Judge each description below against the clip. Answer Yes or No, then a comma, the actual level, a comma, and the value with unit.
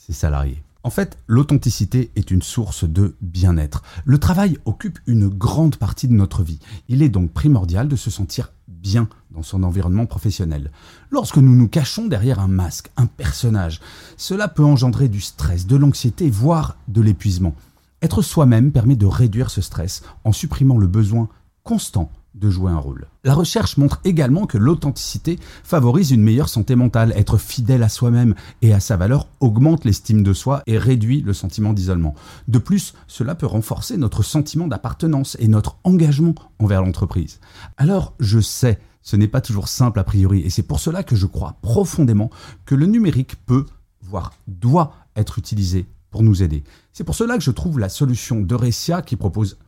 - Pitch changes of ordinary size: No, wide, 5.7 semitones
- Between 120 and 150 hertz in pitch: No, low, 110 Hz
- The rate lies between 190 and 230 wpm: No, average, 175 wpm